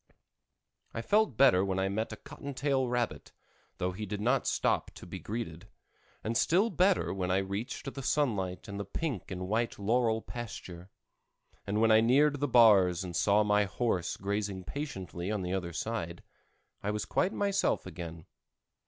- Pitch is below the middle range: Yes, low, 105 Hz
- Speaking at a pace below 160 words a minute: No, average, 170 wpm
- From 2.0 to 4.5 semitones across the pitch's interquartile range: No, average, 4.9 semitones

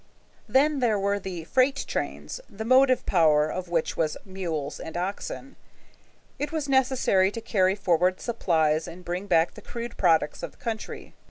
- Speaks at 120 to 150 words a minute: No, average, 165 wpm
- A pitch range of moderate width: No, wide, 6.1 semitones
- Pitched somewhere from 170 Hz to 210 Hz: Yes, high, 190 Hz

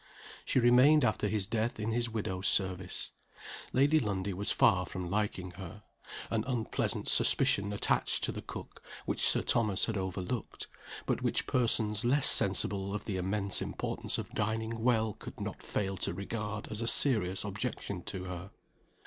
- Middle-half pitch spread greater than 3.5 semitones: No, average, 3.1 semitones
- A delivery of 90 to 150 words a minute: No, average, 165 wpm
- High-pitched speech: No, low, 105 Hz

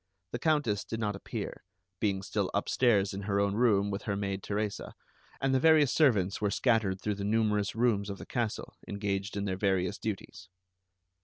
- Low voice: Yes, low, 100 Hz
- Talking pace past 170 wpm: Yes, average, 180 wpm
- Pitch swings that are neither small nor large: No, narrow, 2.3 semitones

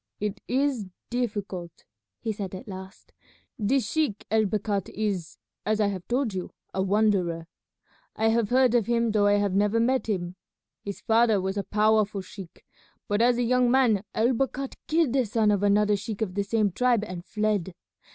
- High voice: Yes, high, 210 Hz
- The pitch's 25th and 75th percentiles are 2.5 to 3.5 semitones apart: Yes, average, 2.9 semitones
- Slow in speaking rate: No, average, 180 wpm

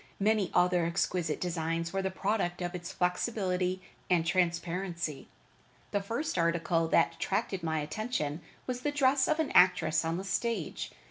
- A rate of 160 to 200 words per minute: No, average, 150 wpm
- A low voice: No, medium, 180 Hz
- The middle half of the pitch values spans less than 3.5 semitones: Yes, average, 2.9 semitones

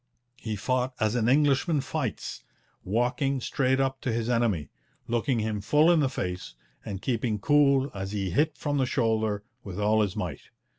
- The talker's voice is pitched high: No, low, 120 Hz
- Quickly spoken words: No, average, 170 wpm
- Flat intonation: No, average, 4.3 semitones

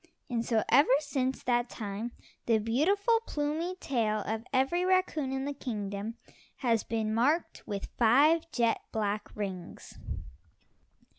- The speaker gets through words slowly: Yes, slow, 130 wpm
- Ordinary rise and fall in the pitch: Yes, average, 5.0 semitones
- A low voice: No, high, 240 Hz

